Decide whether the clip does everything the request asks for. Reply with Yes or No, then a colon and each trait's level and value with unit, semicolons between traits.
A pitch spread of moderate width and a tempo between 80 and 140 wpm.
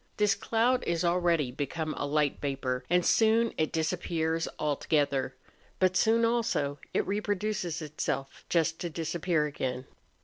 Yes: average, 4.5 semitones; slow, 135 wpm